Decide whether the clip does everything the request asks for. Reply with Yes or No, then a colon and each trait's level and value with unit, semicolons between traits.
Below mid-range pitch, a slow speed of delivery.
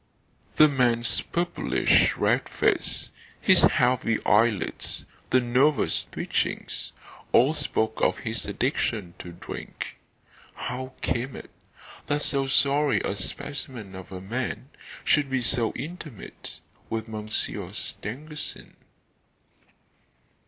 Yes: low, 125 Hz; slow, 105 wpm